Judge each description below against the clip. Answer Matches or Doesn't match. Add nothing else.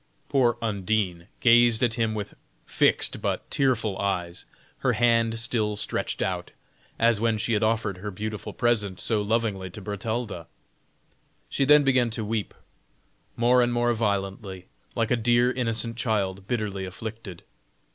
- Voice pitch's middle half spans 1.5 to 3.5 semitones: Matches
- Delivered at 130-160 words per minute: Matches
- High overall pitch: Doesn't match